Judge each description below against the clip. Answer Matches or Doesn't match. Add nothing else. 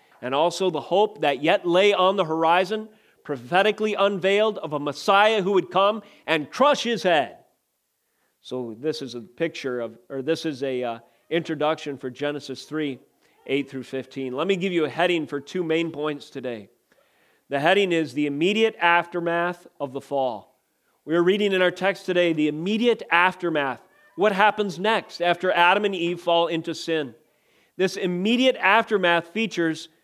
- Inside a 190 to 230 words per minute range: Doesn't match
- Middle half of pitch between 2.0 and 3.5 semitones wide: Doesn't match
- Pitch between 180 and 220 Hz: Doesn't match